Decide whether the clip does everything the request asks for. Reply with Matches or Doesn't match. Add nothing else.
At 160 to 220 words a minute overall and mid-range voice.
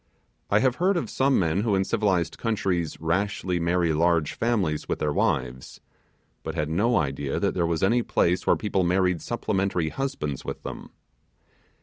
Doesn't match